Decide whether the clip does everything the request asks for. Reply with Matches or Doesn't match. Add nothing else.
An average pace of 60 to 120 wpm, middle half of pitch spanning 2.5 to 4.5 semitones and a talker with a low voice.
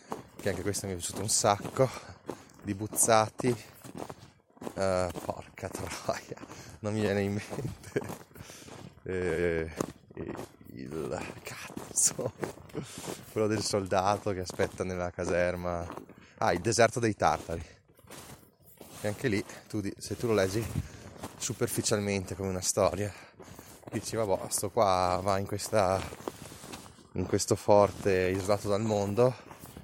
Matches